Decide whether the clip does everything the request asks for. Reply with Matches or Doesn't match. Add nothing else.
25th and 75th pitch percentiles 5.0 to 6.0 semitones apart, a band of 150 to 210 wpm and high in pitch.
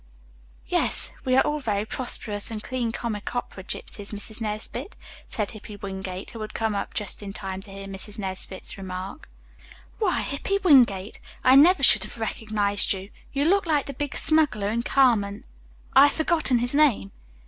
Matches